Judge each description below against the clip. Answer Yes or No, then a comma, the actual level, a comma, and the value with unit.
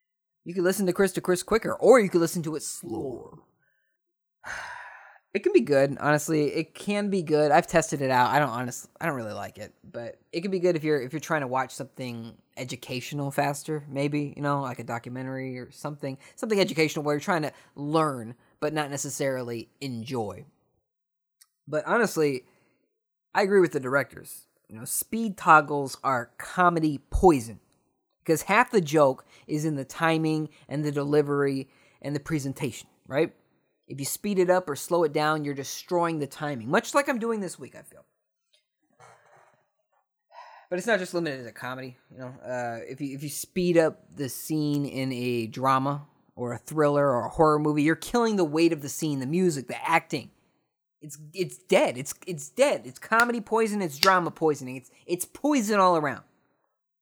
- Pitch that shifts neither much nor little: Yes, average, 4.6 semitones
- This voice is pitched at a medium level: Yes, medium, 150 Hz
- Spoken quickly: No, average, 185 wpm